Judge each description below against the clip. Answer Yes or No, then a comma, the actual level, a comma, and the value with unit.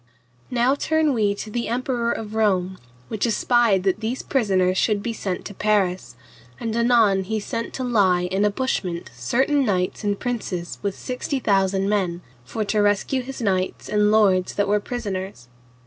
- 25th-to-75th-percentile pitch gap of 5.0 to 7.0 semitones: No, average, 3.8 semitones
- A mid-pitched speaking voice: No, high, 210 Hz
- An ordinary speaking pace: Yes, average, 170 wpm